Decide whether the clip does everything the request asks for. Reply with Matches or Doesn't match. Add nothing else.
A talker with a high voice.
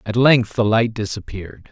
Doesn't match